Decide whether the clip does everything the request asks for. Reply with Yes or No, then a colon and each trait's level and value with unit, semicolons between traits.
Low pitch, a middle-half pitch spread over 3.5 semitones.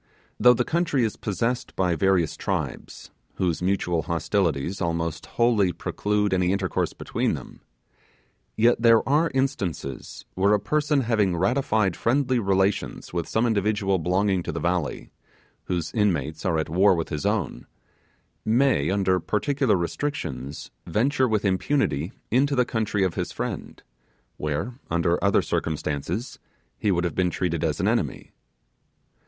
Yes: very low, 95 Hz; average, 5.2 semitones